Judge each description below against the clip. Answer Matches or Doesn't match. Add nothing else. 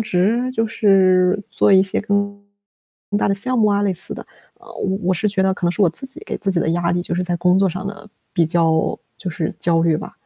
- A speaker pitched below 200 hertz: Matches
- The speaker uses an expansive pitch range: Doesn't match